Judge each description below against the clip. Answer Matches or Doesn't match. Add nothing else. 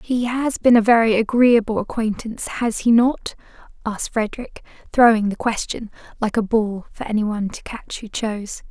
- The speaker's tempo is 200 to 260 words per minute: Doesn't match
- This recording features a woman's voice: Matches